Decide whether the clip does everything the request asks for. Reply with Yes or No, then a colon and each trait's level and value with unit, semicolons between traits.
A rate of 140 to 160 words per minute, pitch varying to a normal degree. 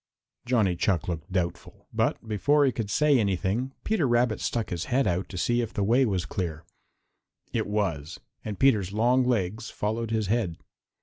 No: average, 175 wpm; average, 4.5 semitones